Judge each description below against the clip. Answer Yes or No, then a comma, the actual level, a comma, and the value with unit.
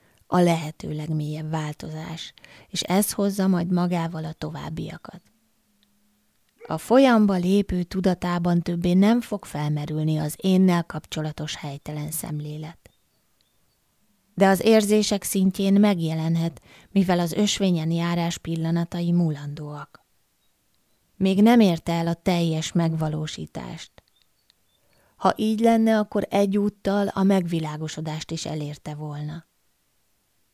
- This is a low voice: No, medium, 175 Hz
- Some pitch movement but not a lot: Yes, average, 4.2 semitones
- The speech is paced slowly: Yes, slow, 100 wpm